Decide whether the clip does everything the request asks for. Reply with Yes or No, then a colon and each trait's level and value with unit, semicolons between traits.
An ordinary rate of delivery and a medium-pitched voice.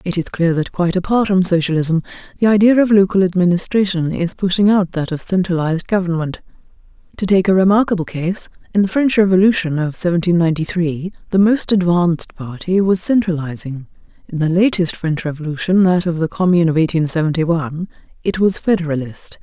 Yes: average, 170 wpm; medium, 175 Hz